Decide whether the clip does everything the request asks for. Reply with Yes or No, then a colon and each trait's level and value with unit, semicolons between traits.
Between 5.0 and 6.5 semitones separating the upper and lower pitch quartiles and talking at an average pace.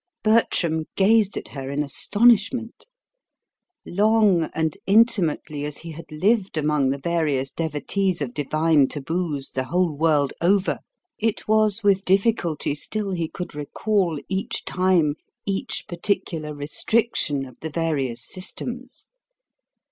No: average, 5.3 semitones; slow, 125 wpm